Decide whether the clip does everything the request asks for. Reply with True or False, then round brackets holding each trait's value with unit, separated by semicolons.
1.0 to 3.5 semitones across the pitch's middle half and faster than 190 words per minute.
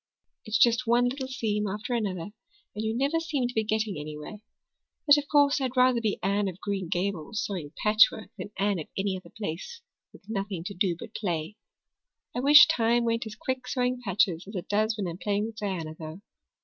False (4.1 semitones; 200 wpm)